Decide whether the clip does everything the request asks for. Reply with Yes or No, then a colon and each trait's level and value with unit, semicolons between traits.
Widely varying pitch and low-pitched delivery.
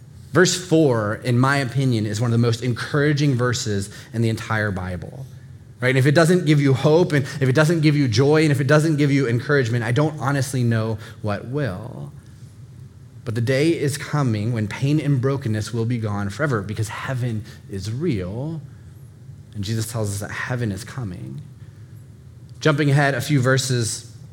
No: average, 3.7 semitones; low, 125 Hz